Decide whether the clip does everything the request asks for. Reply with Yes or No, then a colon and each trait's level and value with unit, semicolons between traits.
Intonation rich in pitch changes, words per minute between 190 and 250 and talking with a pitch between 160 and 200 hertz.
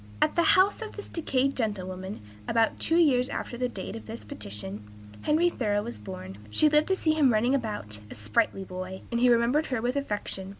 No: wide, 7.2 semitones; fast, 205 wpm; high, 235 Hz